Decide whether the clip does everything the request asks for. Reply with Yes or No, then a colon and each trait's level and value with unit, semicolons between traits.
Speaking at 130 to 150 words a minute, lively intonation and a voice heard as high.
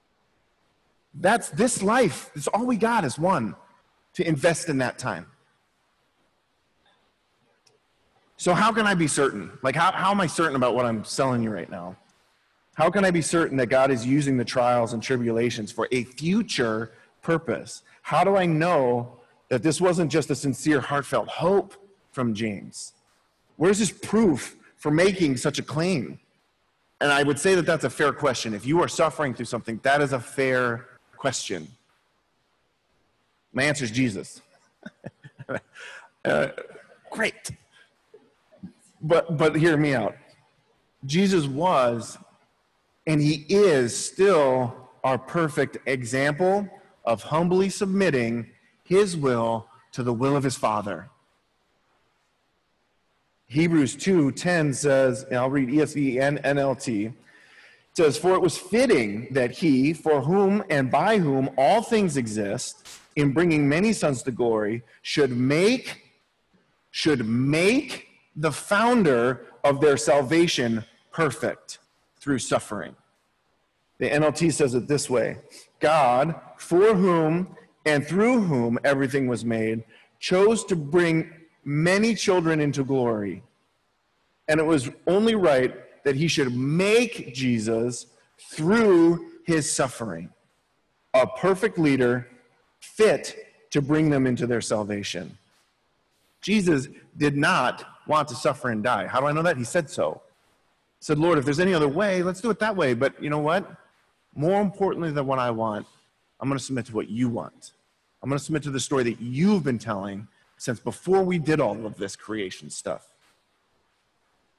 No: average, 145 wpm; wide, 5.9 semitones; medium, 145 Hz